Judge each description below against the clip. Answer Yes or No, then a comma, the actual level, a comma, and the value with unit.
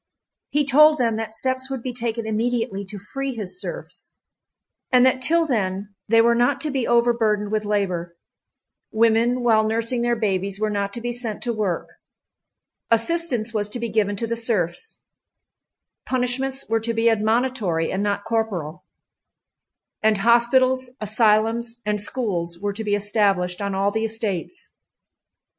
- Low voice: No, high, 225 Hz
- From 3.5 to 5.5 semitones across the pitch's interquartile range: No, average, 2.9 semitones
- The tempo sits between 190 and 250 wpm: No, average, 150 wpm